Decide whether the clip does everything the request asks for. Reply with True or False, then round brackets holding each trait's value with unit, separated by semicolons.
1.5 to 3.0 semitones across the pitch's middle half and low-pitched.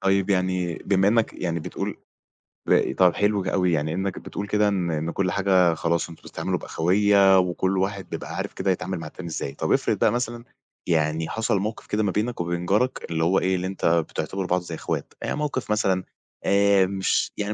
True (2.6 semitones; 95 Hz)